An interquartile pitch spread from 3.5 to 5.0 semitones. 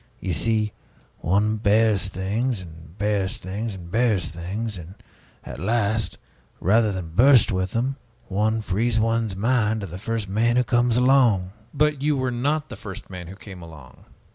Yes: average, 3.8 semitones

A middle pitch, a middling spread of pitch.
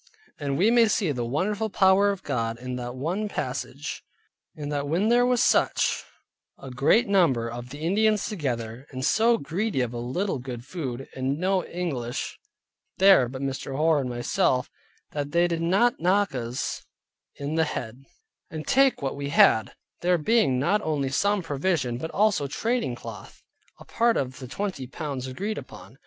No: medium, 150 Hz; wide, 7.3 semitones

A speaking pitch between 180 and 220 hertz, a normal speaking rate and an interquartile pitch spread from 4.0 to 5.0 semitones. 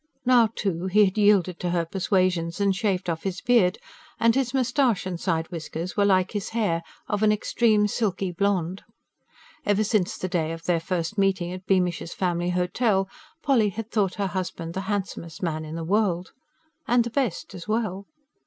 No: high, 190 Hz; average, 180 wpm; average, 3.2 semitones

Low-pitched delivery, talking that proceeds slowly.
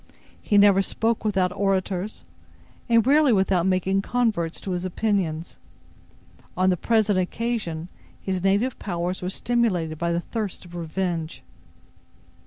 No: high, 190 Hz; slow, 130 wpm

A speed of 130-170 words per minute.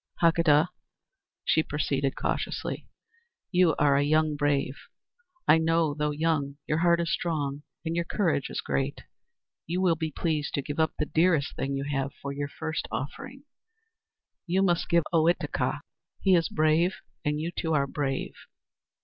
Yes: average, 160 wpm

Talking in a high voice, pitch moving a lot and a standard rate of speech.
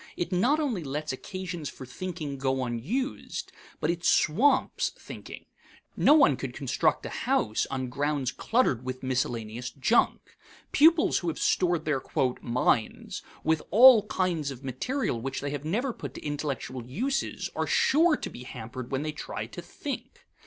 No: medium, 150 Hz; wide, 8.0 semitones; average, 160 wpm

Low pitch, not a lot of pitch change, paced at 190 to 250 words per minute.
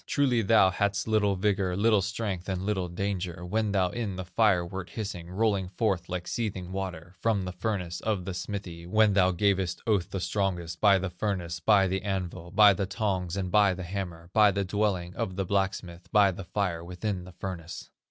Yes: very low, 95 Hz; narrow, 2.3 semitones; average, 195 wpm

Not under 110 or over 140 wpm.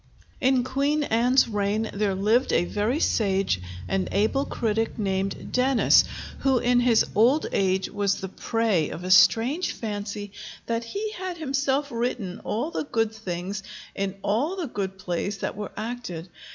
No: average, 155 wpm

